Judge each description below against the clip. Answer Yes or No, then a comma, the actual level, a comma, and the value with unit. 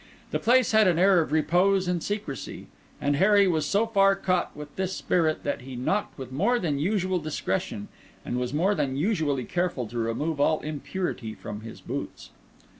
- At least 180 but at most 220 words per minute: Yes, average, 185 wpm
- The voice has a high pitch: No, medium, 170 Hz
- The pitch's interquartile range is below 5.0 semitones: No, wide, 5.6 semitones